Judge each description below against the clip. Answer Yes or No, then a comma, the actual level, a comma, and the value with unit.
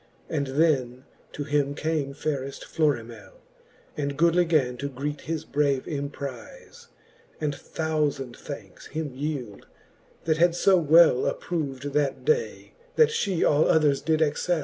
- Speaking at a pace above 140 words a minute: No, slow, 135 wpm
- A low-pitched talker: No, medium, 150 Hz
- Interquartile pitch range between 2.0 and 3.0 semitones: Yes, narrow, 2.6 semitones